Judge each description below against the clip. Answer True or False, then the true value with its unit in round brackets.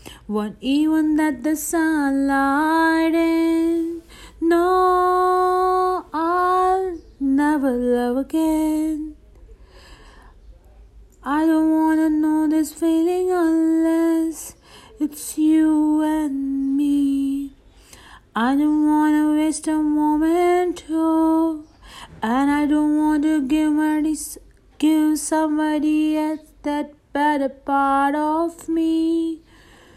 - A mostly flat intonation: True (1.6 semitones)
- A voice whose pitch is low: False (310 Hz)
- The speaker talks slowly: True (85 wpm)